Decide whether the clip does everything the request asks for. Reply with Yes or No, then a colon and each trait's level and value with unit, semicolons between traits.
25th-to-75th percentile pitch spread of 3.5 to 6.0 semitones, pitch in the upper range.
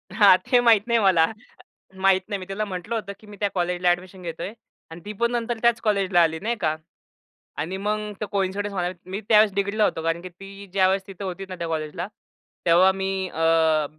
No: average, 2.9 semitones; high, 195 Hz